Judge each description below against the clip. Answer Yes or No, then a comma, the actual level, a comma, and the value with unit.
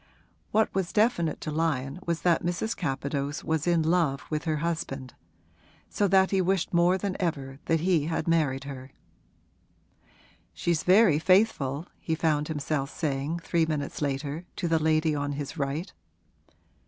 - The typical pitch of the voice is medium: Yes, medium, 160 Hz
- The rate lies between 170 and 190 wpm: No, average, 155 wpm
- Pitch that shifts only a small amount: No, average, 3.4 semitones